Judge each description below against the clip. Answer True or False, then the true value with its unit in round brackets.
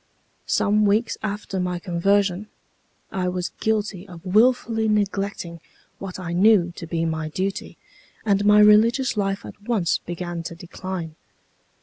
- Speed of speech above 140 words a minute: False (135 wpm)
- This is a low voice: False (195 Hz)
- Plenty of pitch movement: False (3.2 semitones)